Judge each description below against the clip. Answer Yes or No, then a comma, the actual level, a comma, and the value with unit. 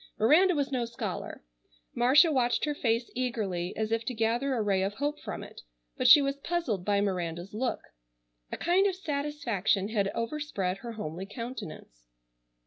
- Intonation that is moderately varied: No, wide, 6.0 semitones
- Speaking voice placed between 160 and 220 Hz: No, high, 235 Hz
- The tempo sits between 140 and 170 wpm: Yes, average, 165 wpm